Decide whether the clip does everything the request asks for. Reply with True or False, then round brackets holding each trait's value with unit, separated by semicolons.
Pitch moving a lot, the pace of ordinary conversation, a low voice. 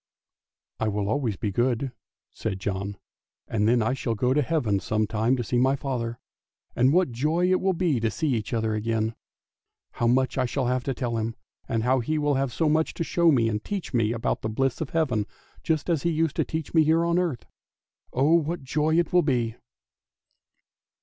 False (5.8 semitones; 215 wpm; 130 Hz)